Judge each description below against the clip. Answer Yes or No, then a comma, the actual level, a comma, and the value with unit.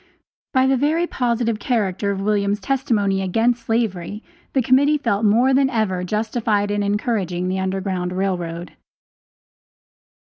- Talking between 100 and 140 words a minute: Yes, slow, 135 wpm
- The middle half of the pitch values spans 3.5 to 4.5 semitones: Yes, average, 4.0 semitones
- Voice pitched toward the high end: Yes, high, 210 Hz